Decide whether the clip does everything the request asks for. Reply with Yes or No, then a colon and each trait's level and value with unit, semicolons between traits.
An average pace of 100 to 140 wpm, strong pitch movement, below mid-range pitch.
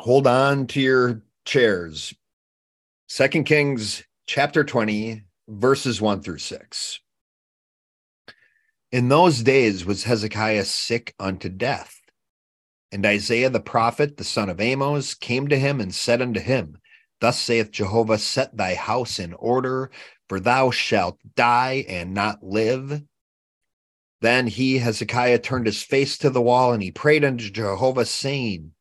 No: slow, 135 wpm; average, 4.3 semitones; low, 120 Hz